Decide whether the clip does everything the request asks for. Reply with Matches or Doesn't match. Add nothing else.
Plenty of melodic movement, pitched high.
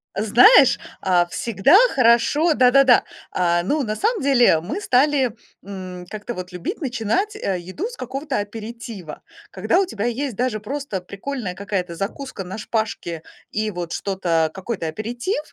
Matches